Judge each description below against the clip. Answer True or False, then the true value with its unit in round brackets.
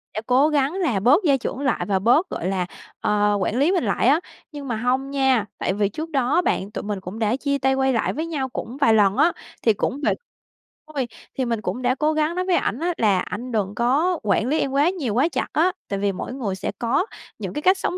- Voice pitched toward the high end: True (260 Hz)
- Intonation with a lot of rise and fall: True (5.9 semitones)